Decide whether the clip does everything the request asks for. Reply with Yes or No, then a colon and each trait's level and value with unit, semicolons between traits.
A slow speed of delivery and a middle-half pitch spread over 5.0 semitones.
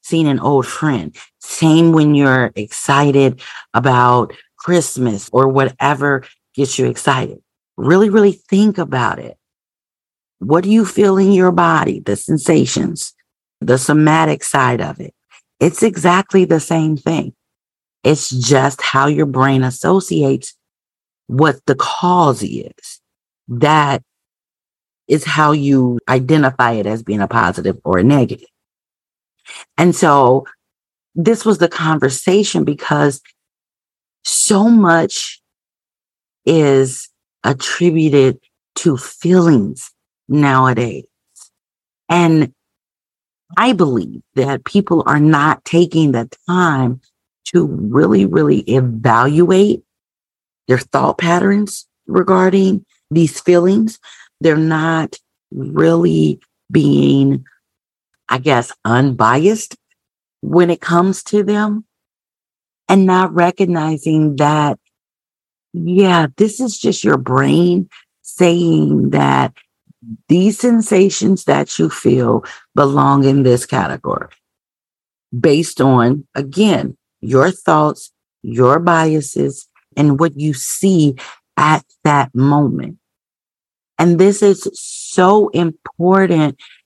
Yes: slow, 100 wpm; wide, 5.4 semitones